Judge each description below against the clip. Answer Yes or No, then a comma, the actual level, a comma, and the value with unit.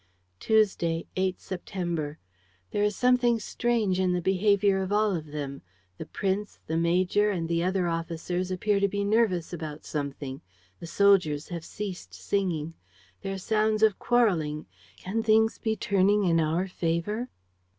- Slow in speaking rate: No, average, 150 wpm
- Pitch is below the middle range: No, medium, 185 Hz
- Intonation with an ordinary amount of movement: Yes, average, 3.8 semitones